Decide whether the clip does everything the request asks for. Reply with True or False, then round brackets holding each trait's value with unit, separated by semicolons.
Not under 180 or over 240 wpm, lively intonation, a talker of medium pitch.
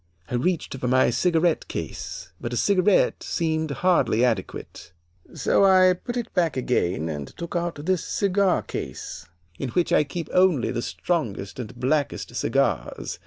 False (155 wpm; 6.7 semitones; 160 Hz)